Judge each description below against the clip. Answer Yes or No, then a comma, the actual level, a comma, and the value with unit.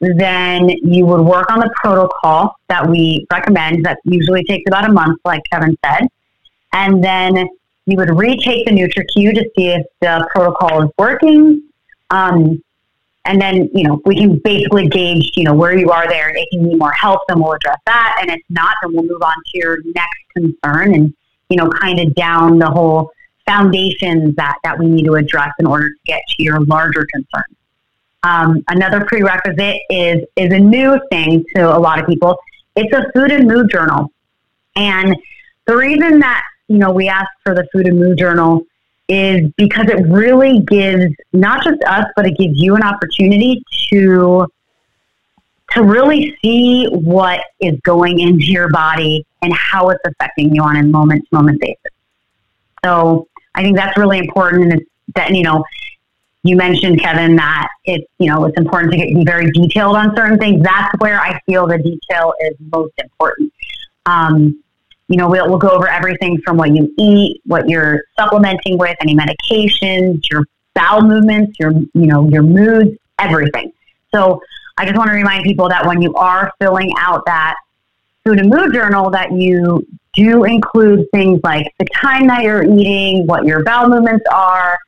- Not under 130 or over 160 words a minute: No, average, 180 wpm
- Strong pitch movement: No, average, 3.5 semitones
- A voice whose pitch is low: No, medium, 180 Hz